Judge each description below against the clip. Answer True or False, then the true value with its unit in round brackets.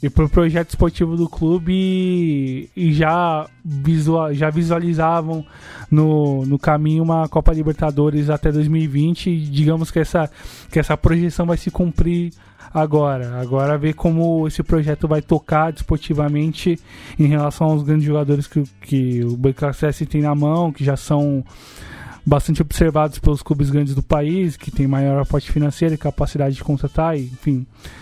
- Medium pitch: True (155 Hz)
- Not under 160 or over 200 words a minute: False (150 wpm)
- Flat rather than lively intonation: True (2.1 semitones)